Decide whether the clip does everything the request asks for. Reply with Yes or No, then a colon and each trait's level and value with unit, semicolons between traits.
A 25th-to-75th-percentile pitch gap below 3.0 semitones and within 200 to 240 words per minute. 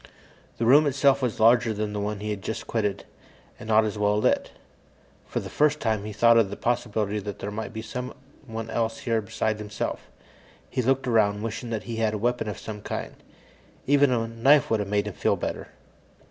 Yes: narrow, 2.6 semitones; fast, 205 wpm